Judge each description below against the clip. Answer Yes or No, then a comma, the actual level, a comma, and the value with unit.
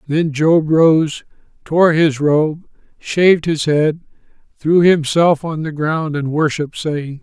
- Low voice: No, medium, 155 Hz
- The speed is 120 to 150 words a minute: Yes, average, 140 wpm